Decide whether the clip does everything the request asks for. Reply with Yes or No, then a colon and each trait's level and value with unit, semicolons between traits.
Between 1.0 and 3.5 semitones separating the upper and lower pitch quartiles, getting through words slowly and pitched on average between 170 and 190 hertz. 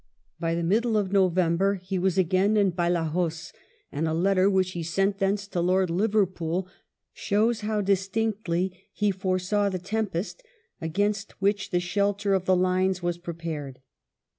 No: narrow, 2.5 semitones; average, 150 wpm; medium, 185 Hz